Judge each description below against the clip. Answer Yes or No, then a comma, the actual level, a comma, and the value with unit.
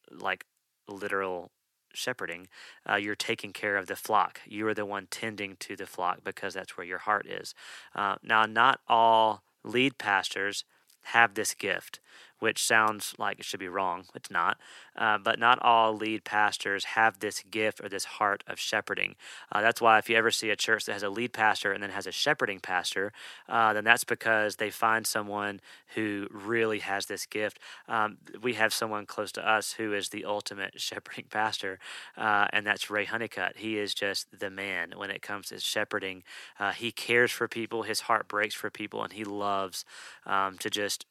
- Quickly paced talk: No, average, 195 wpm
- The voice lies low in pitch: Yes, low, 105 Hz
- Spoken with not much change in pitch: Yes, narrow, 1.8 semitones